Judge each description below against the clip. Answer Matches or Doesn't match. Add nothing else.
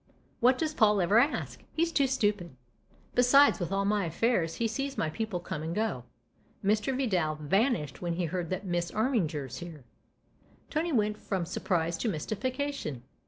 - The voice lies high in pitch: Matches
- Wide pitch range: Matches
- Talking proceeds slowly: Doesn't match